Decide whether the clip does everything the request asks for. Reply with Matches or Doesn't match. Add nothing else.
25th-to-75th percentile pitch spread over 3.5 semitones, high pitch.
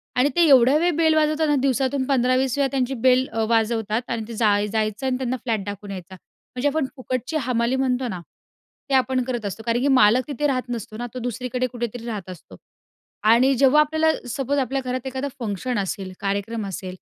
Doesn't match